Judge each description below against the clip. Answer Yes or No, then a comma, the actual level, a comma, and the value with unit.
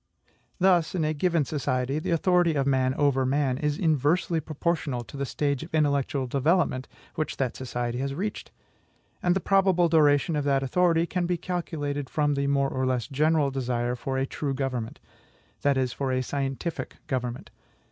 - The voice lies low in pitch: No, medium, 145 Hz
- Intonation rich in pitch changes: No, average, 3.6 semitones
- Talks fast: No, average, 175 wpm